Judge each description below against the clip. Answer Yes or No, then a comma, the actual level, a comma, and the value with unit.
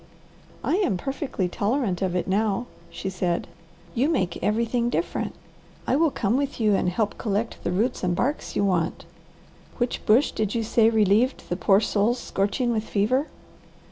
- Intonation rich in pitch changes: No, average, 4.2 semitones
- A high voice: Yes, high, 215 Hz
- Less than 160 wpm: No, average, 170 wpm